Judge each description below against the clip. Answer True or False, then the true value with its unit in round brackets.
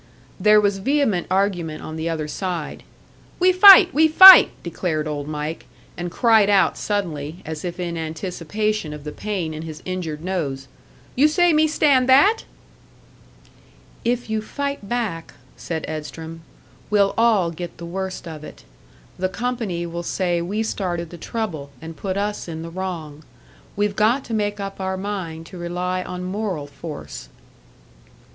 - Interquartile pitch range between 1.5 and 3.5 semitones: False (4.7 semitones)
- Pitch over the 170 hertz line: True (185 Hz)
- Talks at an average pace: True (155 wpm)